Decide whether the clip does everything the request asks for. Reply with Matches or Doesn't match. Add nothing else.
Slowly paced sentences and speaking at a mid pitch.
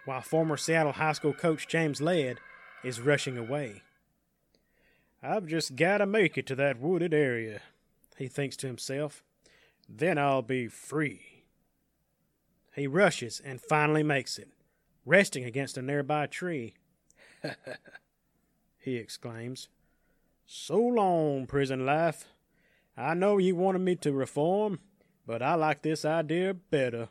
Matches